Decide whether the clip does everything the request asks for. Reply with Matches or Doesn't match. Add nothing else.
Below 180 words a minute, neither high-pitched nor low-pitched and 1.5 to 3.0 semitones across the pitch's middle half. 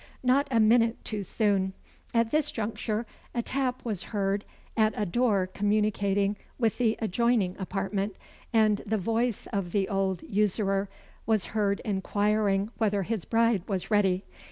Doesn't match